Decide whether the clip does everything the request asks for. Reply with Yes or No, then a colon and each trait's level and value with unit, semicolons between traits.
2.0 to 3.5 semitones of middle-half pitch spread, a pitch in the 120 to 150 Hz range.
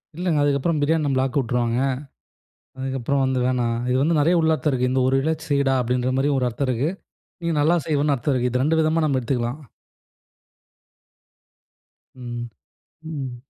Yes: average, 3.2 semitones; low, 135 Hz